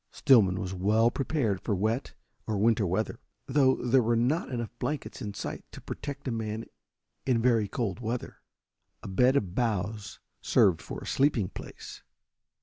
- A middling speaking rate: Yes, average, 160 wpm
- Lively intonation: No, average, 3.7 semitones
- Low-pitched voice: Yes, low, 115 Hz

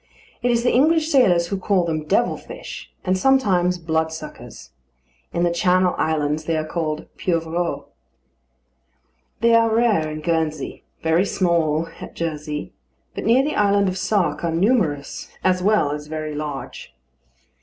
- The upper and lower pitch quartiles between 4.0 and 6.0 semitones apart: Yes, average, 4.5 semitones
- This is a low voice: No, medium, 170 Hz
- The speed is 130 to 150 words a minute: Yes, average, 145 wpm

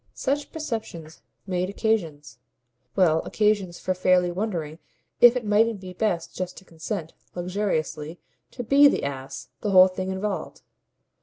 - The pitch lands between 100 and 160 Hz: No, medium, 185 Hz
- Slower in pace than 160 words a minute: Yes, average, 140 wpm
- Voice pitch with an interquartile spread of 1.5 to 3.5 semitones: No, average, 4.1 semitones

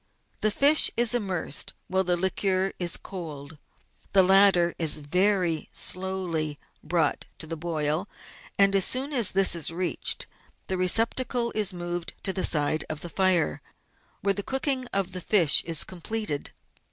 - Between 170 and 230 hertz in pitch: Yes, medium, 185 Hz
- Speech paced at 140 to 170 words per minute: Yes, average, 150 wpm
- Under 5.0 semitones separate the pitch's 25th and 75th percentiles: Yes, average, 3.2 semitones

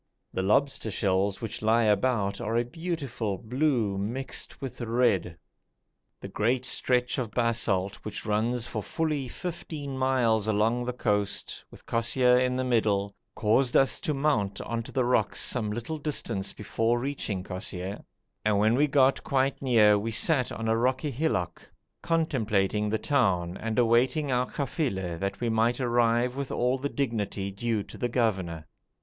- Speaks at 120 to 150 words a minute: No, average, 160 wpm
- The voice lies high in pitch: No, low, 115 Hz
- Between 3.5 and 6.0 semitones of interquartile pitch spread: Yes, average, 3.8 semitones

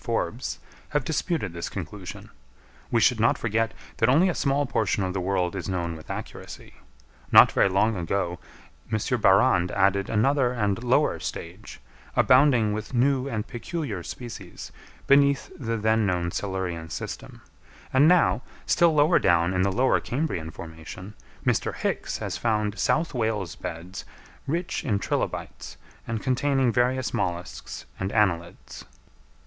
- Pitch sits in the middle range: No, low, 110 Hz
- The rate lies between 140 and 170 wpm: Yes, average, 145 wpm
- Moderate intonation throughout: No, wide, 5.8 semitones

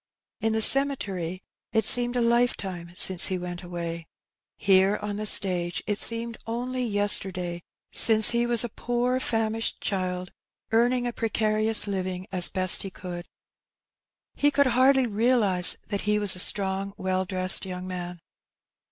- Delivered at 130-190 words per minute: Yes, average, 150 wpm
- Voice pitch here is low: No, high, 205 Hz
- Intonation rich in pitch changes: No, average, 4.1 semitones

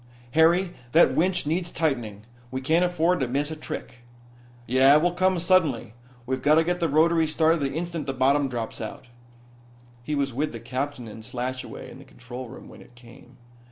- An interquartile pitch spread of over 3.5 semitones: Yes, average, 4.7 semitones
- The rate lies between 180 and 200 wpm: Yes, average, 190 wpm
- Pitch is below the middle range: No, medium, 145 Hz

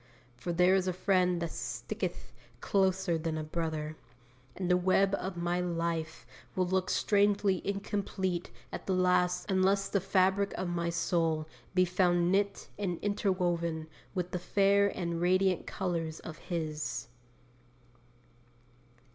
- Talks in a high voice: No, medium, 180 Hz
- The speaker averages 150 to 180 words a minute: No, slow, 135 wpm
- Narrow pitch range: Yes, narrow, 2.1 semitones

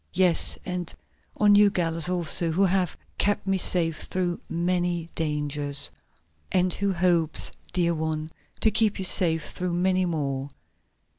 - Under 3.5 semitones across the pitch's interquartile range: Yes, narrow, 2.4 semitones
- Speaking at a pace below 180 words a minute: Yes, average, 145 wpm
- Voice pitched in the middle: Yes, medium, 175 Hz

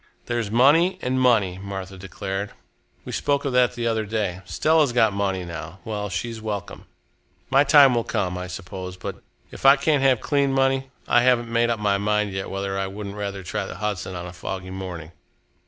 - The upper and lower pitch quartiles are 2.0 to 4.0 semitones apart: No, average, 4.6 semitones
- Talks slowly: No, average, 195 wpm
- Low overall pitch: Yes, low, 105 Hz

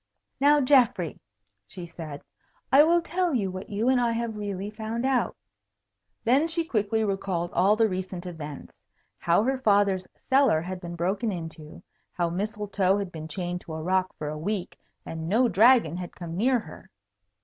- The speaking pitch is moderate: No, high, 200 Hz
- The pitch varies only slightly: No, average, 5.2 semitones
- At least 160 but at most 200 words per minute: Yes, average, 170 wpm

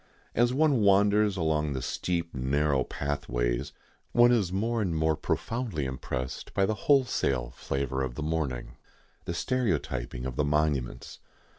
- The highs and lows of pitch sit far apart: Yes, wide, 7.6 semitones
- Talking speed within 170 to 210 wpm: No, average, 140 wpm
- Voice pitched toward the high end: No, very low, 75 Hz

